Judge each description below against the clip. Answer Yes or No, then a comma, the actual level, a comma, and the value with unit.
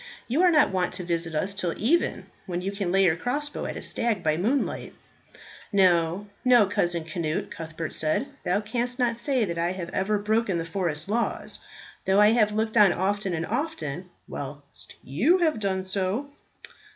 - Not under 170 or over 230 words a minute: Yes, average, 180 wpm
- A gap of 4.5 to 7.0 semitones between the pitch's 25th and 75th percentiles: Yes, average, 5.1 semitones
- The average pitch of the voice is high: Yes, high, 195 Hz